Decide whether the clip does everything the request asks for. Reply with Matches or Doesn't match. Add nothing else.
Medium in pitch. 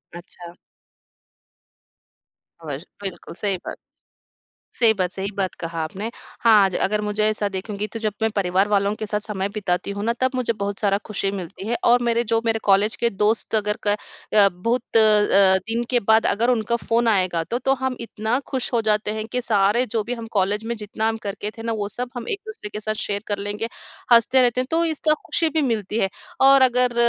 Doesn't match